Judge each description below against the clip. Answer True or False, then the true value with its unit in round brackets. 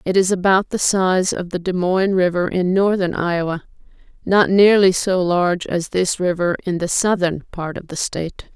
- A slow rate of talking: False (190 wpm)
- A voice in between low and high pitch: True (180 Hz)